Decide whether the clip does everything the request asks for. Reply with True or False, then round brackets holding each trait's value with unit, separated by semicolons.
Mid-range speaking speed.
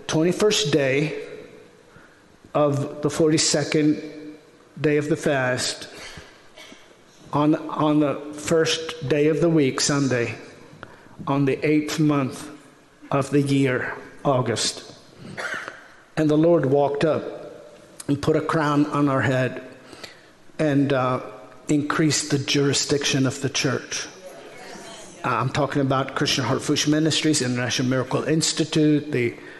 False (115 wpm)